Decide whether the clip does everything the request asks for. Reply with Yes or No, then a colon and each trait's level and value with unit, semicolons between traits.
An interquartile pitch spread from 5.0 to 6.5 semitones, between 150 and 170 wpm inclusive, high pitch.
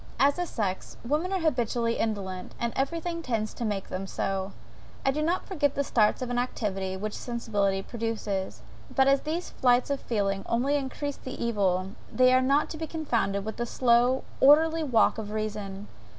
No: average, 5.3 semitones; average, 180 wpm; high, 235 Hz